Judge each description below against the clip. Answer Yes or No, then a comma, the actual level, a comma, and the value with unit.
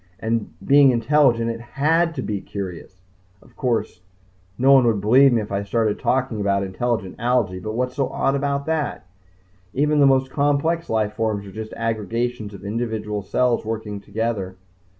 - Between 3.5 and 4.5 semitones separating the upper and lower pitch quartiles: Yes, average, 4.2 semitones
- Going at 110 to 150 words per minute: No, average, 170 wpm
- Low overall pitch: Yes, low, 115 Hz